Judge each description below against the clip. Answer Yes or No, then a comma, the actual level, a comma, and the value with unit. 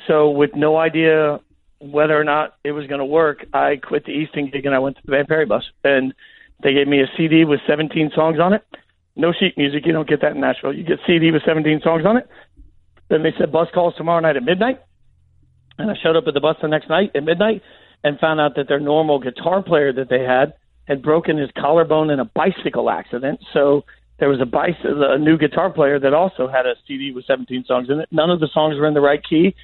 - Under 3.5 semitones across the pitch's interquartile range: Yes, narrow, 2.5 semitones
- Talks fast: Yes, fast, 245 wpm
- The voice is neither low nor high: Yes, medium, 150 Hz